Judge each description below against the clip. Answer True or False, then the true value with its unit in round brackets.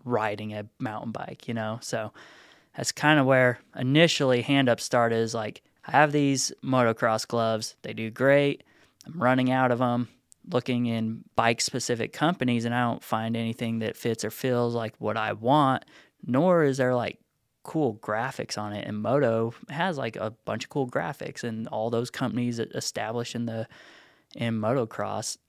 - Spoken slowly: False (175 wpm)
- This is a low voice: True (120 Hz)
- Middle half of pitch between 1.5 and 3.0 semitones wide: True (2.4 semitones)